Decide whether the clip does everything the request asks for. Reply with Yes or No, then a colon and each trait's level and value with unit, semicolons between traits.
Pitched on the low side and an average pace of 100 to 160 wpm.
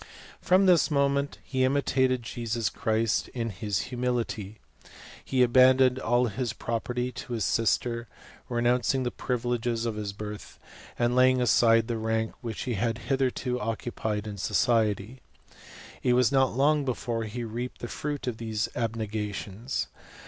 Yes: low, 120 Hz; average, 150 wpm